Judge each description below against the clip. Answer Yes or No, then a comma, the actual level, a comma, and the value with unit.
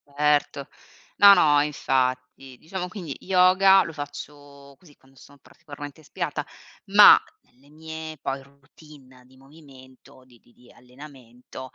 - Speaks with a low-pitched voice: No, medium, 145 Hz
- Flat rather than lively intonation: No, average, 3.2 semitones